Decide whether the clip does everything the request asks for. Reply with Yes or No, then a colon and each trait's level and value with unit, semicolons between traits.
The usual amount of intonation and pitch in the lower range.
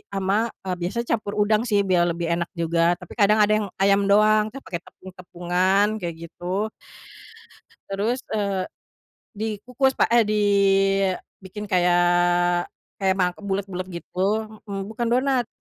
No: average, 3.1 semitones; high, 195 Hz